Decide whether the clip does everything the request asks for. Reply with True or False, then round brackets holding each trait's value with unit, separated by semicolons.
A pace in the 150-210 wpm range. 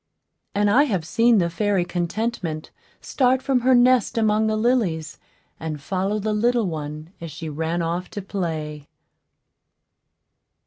False (140 wpm)